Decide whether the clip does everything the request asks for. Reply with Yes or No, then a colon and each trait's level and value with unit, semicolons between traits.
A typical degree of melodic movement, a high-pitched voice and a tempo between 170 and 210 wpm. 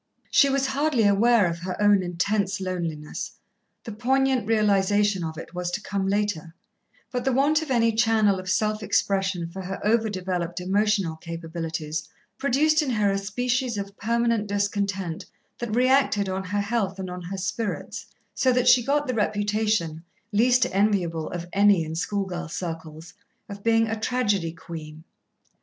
No: average, 4.2 semitones; high, 200 Hz; average, 160 wpm